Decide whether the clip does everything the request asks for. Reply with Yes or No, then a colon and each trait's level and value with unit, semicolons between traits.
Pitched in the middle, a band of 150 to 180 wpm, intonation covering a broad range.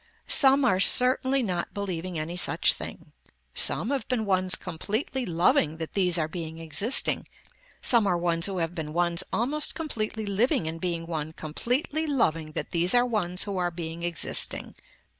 Yes: medium, 180 Hz; average, 165 wpm; wide, 6.0 semitones